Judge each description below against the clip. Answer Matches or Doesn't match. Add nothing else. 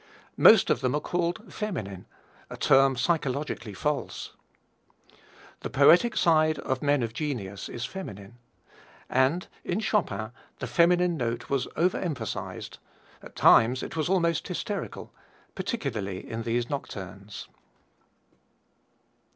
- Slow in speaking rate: Matches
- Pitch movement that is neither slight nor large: Doesn't match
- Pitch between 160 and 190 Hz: Doesn't match